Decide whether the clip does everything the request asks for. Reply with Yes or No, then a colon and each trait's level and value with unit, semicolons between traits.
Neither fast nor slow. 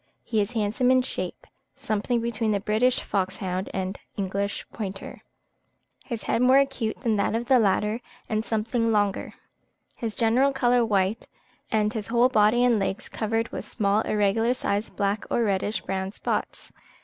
Yes: average, 160 wpm